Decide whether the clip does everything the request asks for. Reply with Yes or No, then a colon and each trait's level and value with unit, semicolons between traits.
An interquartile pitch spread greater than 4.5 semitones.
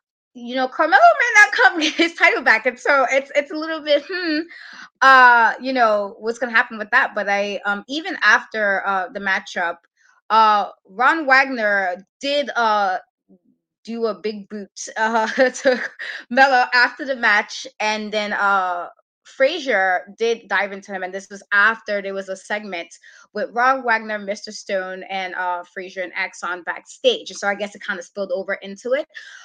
Yes: average, 5.3 semitones